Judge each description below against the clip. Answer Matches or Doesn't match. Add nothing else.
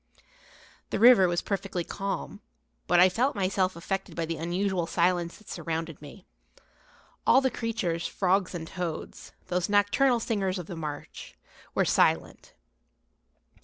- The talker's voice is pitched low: Doesn't match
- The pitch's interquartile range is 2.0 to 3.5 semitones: Matches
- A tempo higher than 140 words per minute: Doesn't match